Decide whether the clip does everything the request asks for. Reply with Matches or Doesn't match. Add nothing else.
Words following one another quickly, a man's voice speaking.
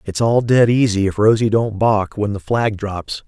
Matches